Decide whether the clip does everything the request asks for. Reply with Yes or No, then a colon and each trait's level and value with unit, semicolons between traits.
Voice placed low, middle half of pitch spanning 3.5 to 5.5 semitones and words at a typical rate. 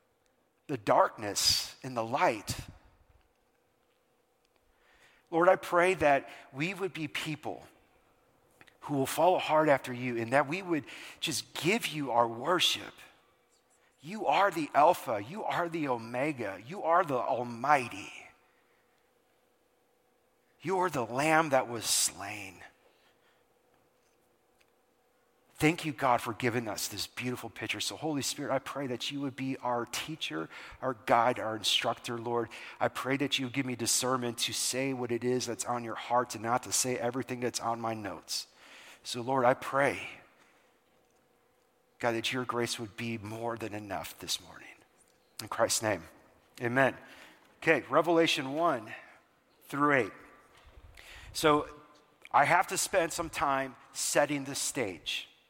Yes: low, 130 Hz; average, 4.9 semitones; average, 145 wpm